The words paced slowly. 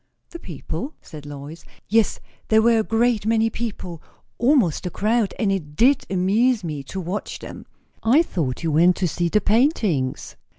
No: average, 170 wpm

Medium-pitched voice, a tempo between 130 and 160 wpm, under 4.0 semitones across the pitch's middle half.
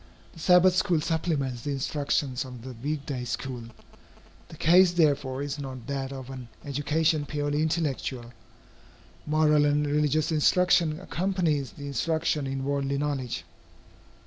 Yes: medium, 145 Hz; slow, 135 wpm; average, 2.9 semitones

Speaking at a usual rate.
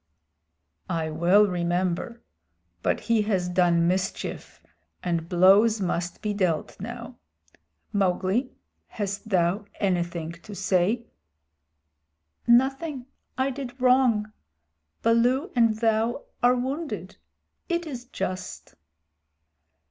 No: slow, 95 wpm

